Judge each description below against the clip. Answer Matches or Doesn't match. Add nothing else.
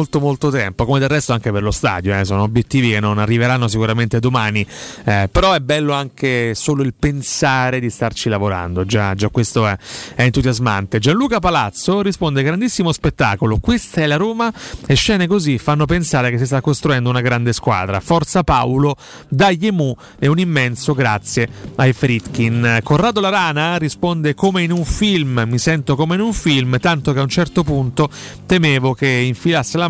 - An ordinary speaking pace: Doesn't match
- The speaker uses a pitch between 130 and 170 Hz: Matches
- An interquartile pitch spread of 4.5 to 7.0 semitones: Matches